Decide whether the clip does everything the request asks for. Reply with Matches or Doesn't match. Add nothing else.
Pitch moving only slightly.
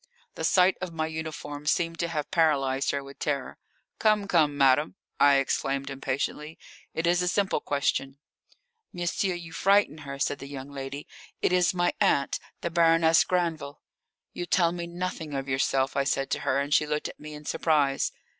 Doesn't match